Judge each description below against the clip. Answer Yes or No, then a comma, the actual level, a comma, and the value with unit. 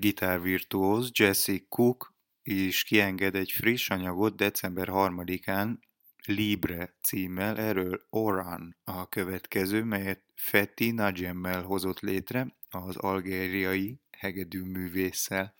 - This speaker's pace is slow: Yes, slow, 95 wpm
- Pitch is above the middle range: No, very low, 95 Hz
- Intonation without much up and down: Yes, narrow, 1.9 semitones